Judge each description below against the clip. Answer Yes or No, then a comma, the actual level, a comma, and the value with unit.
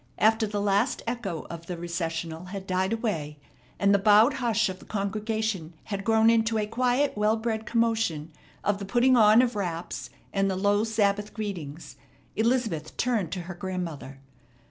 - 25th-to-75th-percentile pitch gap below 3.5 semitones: No, average, 3.8 semitones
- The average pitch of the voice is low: No, high, 205 Hz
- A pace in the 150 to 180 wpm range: Yes, average, 165 wpm